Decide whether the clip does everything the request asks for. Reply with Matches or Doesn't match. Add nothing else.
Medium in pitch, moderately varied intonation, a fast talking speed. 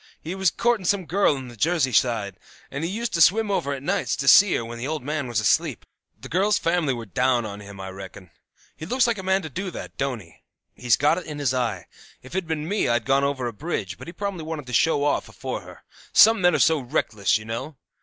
Doesn't match